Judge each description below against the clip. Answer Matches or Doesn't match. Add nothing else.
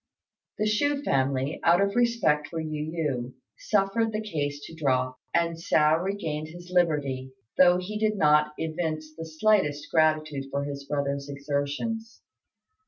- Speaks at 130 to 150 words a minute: Matches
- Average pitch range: Matches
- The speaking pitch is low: Doesn't match